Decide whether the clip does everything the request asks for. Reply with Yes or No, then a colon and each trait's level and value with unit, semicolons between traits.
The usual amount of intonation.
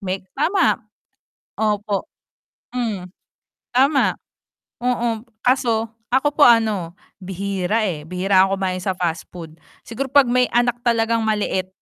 Yes: average, 4.5 semitones